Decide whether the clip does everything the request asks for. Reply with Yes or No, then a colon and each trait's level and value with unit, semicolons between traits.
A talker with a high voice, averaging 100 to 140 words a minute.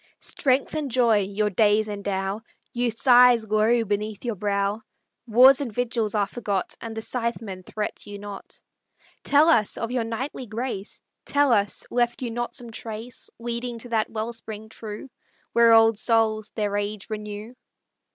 No: high, 225 Hz; average, 155 wpm